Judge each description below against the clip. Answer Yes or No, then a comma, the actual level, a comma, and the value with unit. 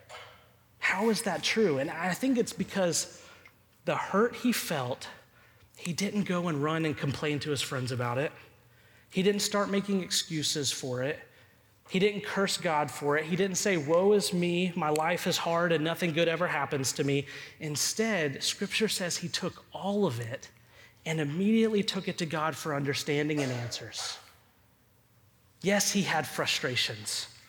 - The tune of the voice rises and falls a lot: Yes, wide, 5.8 semitones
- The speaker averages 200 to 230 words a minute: No, average, 170 wpm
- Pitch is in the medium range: Yes, medium, 160 Hz